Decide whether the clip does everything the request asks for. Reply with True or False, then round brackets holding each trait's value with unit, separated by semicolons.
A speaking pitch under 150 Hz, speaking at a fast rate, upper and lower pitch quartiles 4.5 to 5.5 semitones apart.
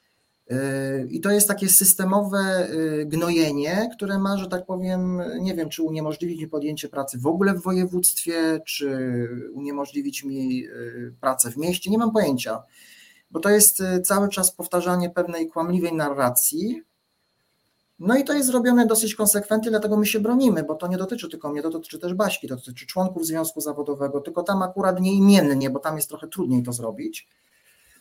False (180 Hz; 165 wpm; 4.9 semitones)